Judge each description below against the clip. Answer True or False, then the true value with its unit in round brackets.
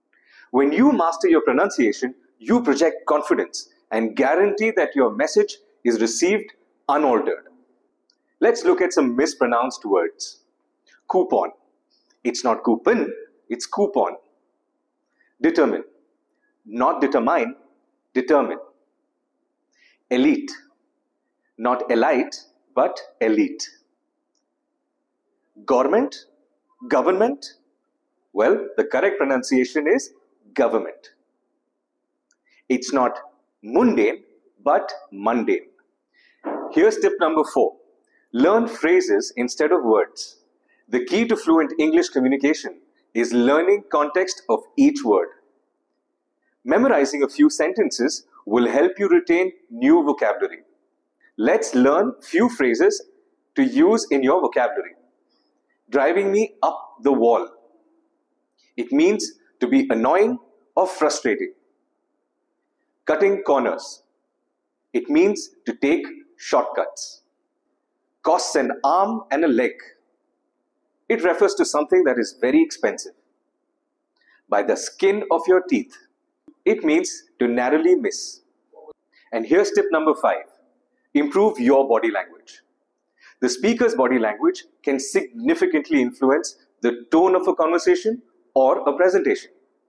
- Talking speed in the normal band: False (105 wpm)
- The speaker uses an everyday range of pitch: False (8.6 semitones)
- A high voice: True (325 Hz)